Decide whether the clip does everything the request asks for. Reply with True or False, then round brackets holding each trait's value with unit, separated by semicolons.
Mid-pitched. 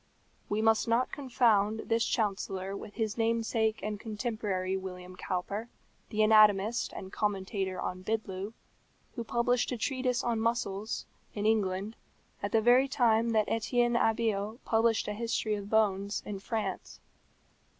False (220 Hz)